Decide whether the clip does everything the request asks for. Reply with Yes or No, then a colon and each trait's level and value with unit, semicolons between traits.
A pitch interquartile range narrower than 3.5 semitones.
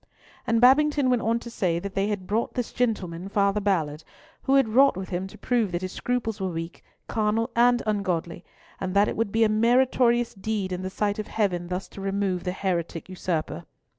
No: average, 3.9 semitones